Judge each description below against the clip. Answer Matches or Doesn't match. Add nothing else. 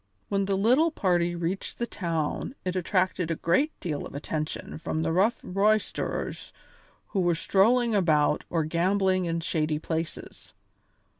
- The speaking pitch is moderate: Matches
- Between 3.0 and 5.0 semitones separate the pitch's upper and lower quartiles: Matches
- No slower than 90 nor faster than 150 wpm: Matches